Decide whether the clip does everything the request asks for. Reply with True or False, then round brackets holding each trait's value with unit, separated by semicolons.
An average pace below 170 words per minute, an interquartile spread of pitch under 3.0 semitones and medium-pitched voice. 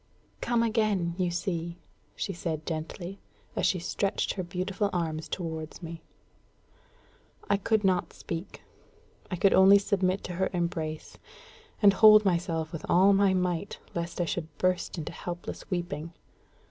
True (145 wpm; 2.6 semitones; 180 Hz)